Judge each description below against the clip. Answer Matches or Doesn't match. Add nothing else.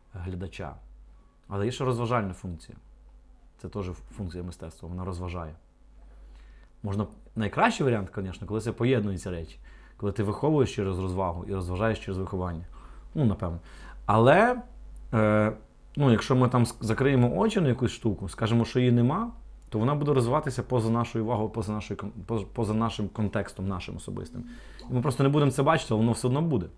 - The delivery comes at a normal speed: Doesn't match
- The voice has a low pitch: Matches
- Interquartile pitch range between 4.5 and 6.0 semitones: Matches